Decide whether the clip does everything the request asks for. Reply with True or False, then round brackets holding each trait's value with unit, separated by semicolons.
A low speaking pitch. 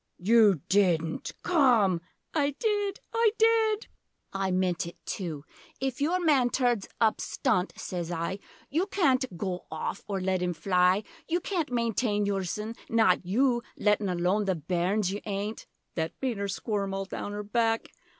False (205 Hz)